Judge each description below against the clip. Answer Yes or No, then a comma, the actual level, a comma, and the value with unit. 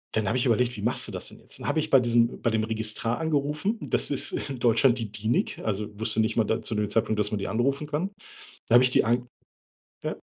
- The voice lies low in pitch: Yes, low, 115 Hz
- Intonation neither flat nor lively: Yes, average, 3.2 semitones